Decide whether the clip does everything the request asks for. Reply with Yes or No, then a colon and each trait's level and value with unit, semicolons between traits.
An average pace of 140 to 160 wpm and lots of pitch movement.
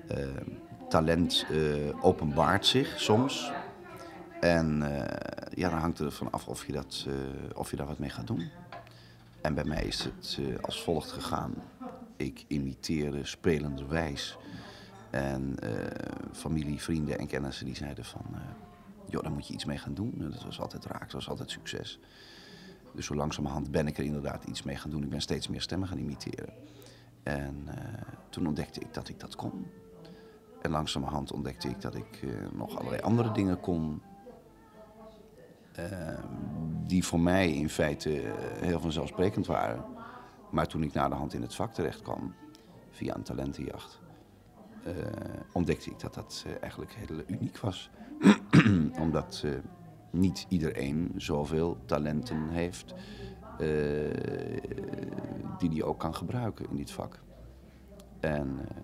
No: average, 155 wpm; average, 3.3 semitones